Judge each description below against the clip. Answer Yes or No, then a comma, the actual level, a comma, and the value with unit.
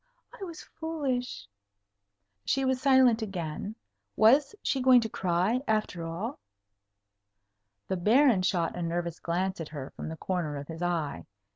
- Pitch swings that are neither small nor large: No, wide, 7.2 semitones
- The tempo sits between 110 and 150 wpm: Yes, average, 145 wpm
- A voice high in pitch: Yes, high, 195 Hz